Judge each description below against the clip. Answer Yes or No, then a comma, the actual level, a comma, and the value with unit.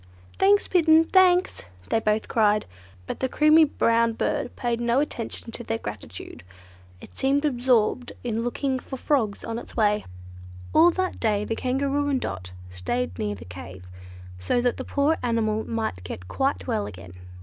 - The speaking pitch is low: No, high, 235 Hz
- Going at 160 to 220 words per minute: Yes, average, 165 wpm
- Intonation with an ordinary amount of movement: Yes, average, 5.0 semitones